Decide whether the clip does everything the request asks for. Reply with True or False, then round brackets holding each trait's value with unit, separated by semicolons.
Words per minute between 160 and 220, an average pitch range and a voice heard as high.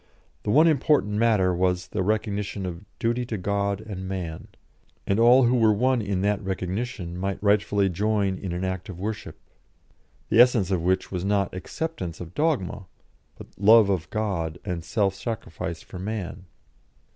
False (165 wpm; 3.0 semitones; 100 Hz)